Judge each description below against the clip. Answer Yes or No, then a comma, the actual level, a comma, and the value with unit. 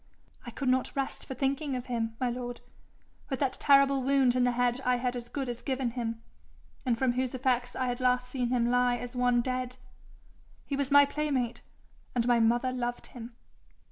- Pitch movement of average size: No, narrow, 1.6 semitones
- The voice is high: Yes, very high, 250 Hz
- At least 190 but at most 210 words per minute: Yes, average, 200 wpm